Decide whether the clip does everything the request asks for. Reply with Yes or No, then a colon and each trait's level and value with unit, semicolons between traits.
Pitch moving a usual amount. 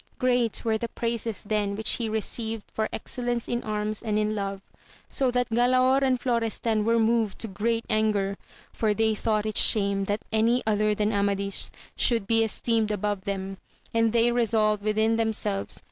No: narrow, 1.8 semitones